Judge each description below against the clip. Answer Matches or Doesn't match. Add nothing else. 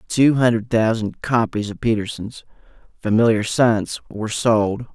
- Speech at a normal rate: Doesn't match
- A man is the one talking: Matches